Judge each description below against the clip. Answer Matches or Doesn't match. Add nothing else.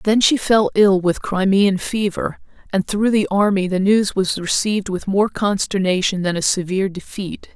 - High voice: Matches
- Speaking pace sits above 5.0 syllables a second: Doesn't match